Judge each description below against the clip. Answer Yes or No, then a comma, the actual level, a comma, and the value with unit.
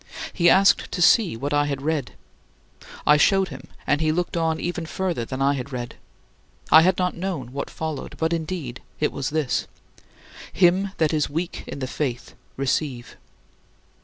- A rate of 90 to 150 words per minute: No, average, 170 wpm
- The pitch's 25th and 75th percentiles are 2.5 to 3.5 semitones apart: No, average, 4.2 semitones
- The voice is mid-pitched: Yes, medium, 155 Hz